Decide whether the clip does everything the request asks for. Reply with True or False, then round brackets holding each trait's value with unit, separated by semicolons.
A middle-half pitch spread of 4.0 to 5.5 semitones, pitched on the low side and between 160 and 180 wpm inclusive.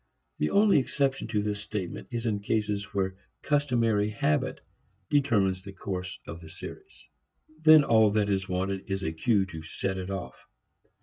False (3.3 semitones; 100 Hz; 165 wpm)